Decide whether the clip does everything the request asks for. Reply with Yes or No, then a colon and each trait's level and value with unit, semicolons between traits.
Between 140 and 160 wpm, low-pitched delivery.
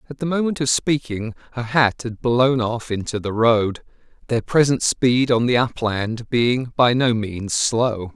No: average, 175 wpm; low, 120 Hz